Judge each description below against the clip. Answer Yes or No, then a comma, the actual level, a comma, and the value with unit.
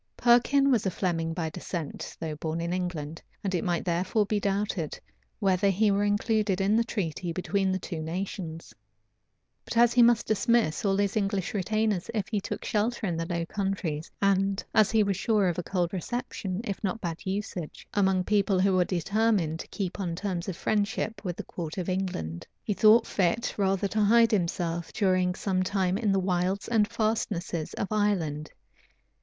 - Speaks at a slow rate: No, average, 185 wpm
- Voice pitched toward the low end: No, high, 195 Hz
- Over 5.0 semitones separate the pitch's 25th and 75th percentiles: No, average, 3.2 semitones